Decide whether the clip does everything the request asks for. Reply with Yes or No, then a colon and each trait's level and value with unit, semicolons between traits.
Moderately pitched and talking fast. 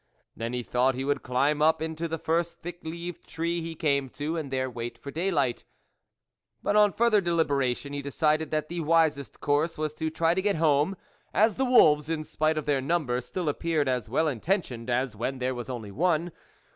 Yes: medium, 155 Hz; fast, 210 wpm